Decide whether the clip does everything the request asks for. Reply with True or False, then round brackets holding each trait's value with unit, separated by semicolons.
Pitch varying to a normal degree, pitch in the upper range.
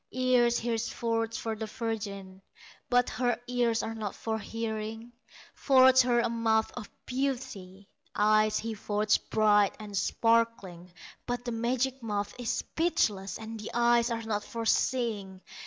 False (2.2 semitones; 225 Hz)